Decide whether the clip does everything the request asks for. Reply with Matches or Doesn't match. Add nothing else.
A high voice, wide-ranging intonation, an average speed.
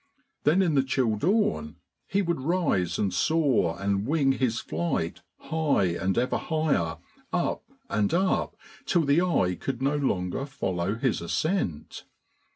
Doesn't match